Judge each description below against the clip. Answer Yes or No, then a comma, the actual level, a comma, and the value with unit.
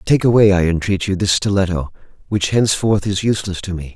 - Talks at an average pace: Yes, average, 195 wpm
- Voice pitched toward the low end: Yes, very low, 95 Hz